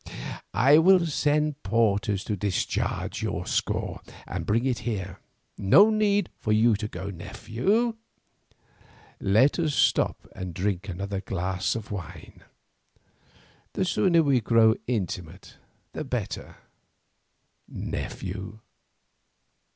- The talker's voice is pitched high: No, low, 110 Hz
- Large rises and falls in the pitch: Yes, wide, 7.3 semitones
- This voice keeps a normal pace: No, slow, 110 wpm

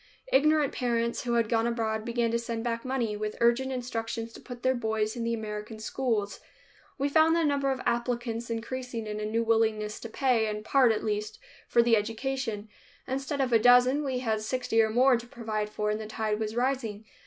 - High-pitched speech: Yes, high, 230 Hz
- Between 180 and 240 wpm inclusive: Yes, fast, 205 wpm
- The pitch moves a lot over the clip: No, narrow, 2.5 semitones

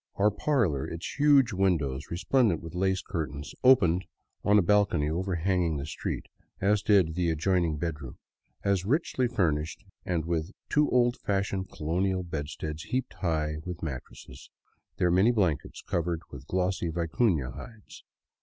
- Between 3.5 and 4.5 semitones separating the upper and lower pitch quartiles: Yes, average, 4.2 semitones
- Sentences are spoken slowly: No, average, 145 wpm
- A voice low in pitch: Yes, very low, 90 Hz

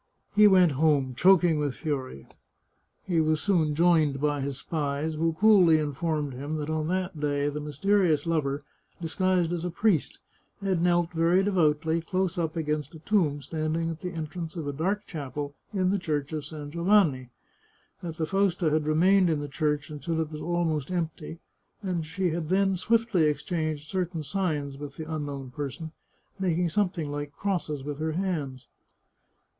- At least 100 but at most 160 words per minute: No, average, 170 wpm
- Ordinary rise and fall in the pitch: Yes, average, 3.2 semitones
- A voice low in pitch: No, medium, 160 Hz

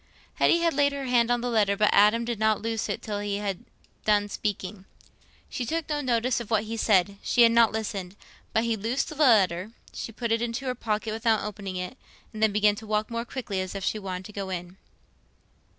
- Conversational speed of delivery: No, fast, 225 wpm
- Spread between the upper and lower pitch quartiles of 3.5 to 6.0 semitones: No, narrow, 2.6 semitones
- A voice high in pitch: Yes, high, 220 Hz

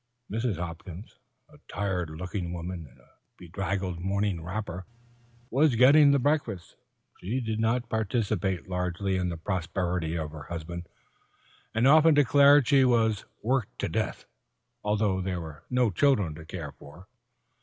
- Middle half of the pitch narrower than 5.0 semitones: No, wide, 5.4 semitones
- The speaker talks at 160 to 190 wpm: No, average, 145 wpm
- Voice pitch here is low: Yes, very low, 95 Hz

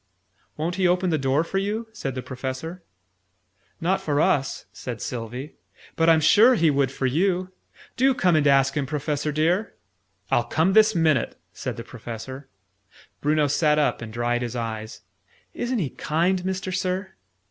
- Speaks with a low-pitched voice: No, medium, 155 Hz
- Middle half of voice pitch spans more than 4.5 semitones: Yes, wide, 5.6 semitones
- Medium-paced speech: Yes, average, 165 wpm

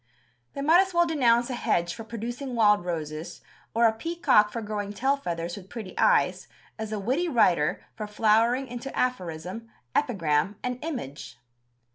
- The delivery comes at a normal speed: Yes, average, 160 wpm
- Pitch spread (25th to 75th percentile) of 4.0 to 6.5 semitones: Yes, average, 5.0 semitones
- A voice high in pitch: Yes, high, 225 Hz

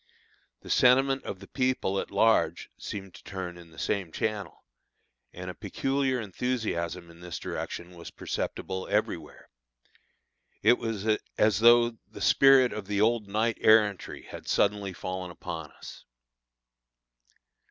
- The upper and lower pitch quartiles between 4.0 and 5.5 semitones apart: Yes, average, 4.4 semitones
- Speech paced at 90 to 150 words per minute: Yes, slow, 135 wpm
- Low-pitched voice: Yes, low, 105 Hz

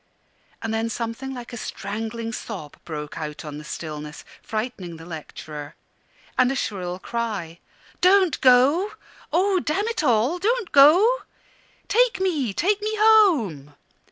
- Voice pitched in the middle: No, high, 235 Hz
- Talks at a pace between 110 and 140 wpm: Yes, slow, 135 wpm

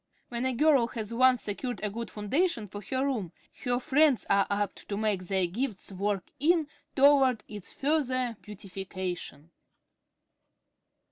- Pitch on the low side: No, high, 230 Hz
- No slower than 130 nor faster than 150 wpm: Yes, average, 140 wpm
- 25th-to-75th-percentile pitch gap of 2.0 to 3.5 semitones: No, average, 4.7 semitones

